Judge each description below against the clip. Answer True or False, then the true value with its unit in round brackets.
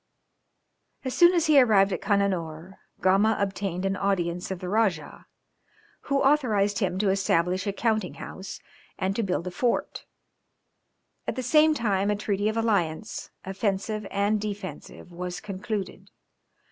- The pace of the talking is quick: False (145 wpm)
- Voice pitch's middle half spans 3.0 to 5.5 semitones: False (2.6 semitones)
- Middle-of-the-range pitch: False (200 Hz)